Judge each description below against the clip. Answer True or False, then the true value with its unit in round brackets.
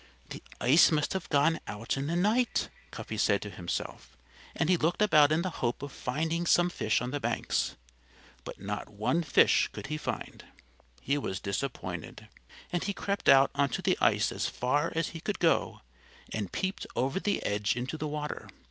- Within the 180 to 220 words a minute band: True (185 wpm)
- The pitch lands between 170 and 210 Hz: False (150 Hz)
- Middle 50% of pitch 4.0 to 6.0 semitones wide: True (5.4 semitones)